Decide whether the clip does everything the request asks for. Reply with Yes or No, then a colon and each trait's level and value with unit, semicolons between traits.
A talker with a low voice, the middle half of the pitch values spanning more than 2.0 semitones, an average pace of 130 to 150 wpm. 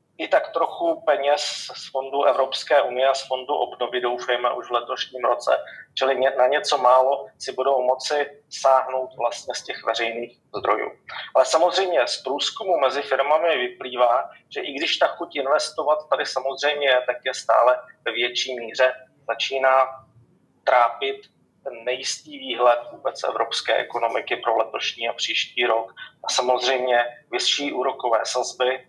Yes: low, 130 Hz; narrow, 2.4 semitones; average, 145 wpm